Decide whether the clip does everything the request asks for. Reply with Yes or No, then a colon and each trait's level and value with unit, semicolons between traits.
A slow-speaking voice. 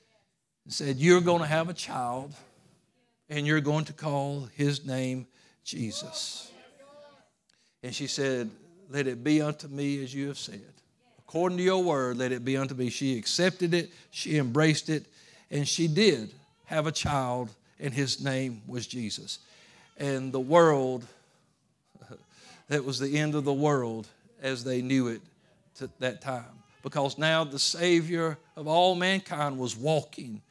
No: average, 155 wpm